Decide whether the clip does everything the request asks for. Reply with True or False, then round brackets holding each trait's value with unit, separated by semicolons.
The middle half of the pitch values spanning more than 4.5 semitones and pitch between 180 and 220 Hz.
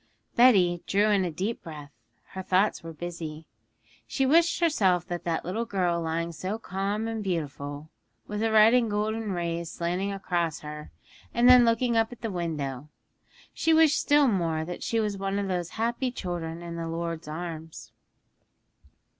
True (5.0 semitones; 185 Hz)